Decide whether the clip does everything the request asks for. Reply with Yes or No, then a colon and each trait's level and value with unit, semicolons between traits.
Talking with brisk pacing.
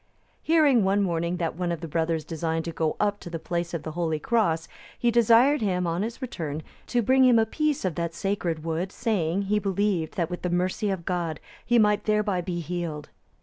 Yes: fast, 215 wpm